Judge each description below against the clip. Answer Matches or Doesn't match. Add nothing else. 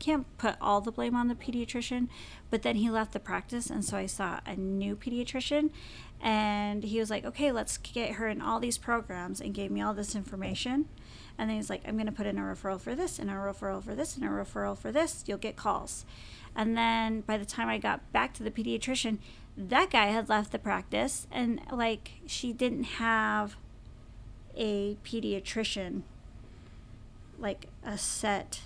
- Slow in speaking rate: Doesn't match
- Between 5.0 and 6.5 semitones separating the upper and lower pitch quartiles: Doesn't match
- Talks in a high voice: Matches